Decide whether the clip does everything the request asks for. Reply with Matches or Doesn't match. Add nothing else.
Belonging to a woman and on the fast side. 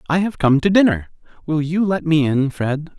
Doesn't match